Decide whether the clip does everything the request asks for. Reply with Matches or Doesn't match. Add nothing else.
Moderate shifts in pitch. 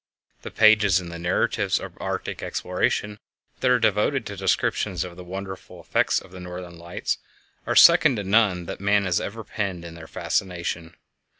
Matches